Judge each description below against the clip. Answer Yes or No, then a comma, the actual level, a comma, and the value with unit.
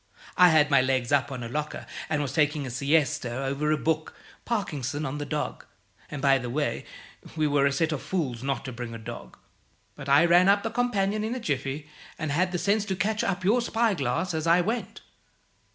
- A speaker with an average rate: No, fast, 215 wpm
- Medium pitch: Yes, medium, 150 Hz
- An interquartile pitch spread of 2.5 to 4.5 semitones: No, average, 5.1 semitones